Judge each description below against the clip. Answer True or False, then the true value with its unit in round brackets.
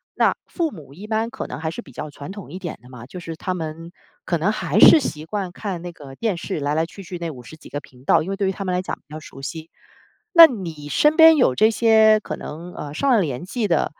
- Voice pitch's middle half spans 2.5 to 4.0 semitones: False (5.5 semitones)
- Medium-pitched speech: True (175 Hz)